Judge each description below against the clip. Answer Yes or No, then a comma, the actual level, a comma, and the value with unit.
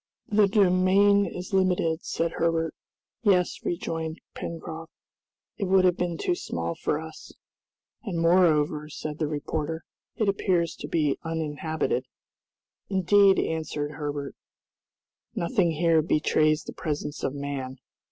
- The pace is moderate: No, slow, 125 wpm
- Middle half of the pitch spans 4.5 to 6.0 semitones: No, average, 3.3 semitones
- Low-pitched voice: No, medium, 165 Hz